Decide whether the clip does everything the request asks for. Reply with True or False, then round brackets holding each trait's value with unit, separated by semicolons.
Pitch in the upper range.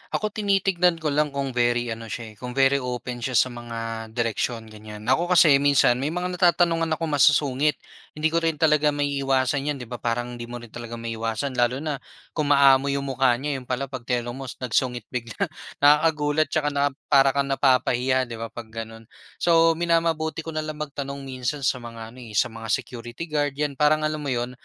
False (135 Hz)